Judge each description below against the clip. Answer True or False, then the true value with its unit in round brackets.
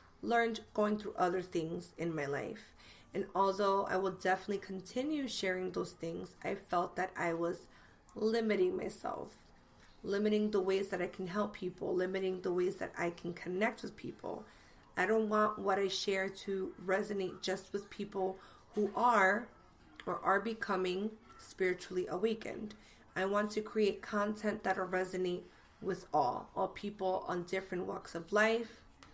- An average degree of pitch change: False (2.3 semitones)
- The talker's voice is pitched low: False (190 Hz)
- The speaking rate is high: False (155 wpm)